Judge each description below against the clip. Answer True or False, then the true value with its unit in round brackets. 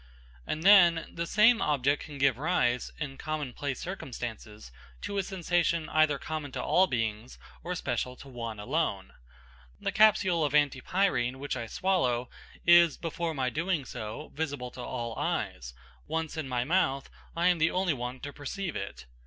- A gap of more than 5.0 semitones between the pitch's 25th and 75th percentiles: True (5.4 semitones)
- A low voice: False (145 Hz)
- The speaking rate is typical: True (165 wpm)